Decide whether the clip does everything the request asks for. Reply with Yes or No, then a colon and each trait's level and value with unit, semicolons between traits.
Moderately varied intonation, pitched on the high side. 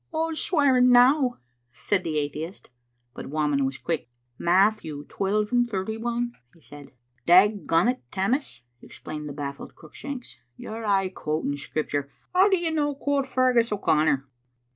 No: wide, 8.6 semitones; high, 205 Hz